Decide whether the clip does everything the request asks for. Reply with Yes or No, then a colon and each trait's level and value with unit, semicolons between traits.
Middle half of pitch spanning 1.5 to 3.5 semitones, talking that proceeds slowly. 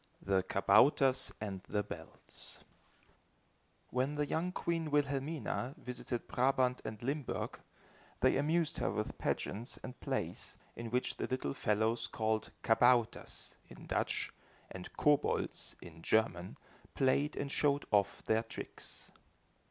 No: average, 4.8 semitones; slow, 120 wpm